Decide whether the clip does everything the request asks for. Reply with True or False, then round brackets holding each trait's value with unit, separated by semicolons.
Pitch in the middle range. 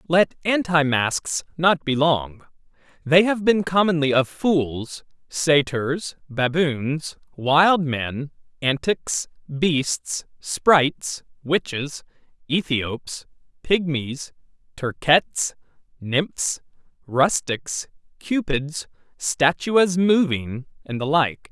True (150 Hz)